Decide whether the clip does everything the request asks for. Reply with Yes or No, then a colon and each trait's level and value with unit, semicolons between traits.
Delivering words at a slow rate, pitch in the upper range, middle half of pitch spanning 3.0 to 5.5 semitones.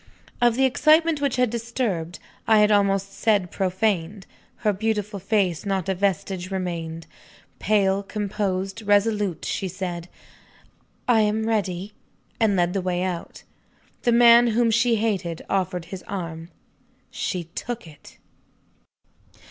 Yes: slow, 130 wpm; high, 200 Hz; average, 3.4 semitones